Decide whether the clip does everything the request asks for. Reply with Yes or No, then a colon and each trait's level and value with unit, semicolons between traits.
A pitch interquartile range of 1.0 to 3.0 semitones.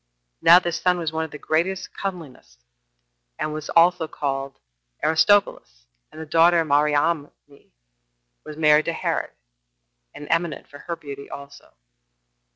Yes: average, 2.7 semitones